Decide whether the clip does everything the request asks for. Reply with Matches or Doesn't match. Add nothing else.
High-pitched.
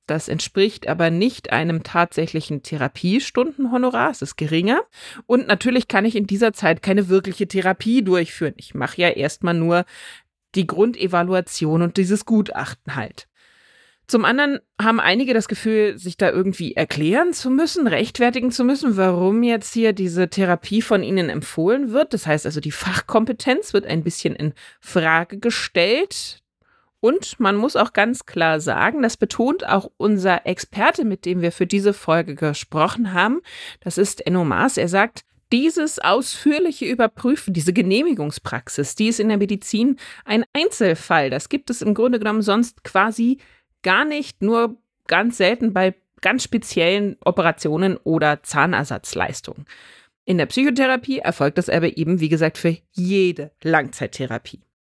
Matches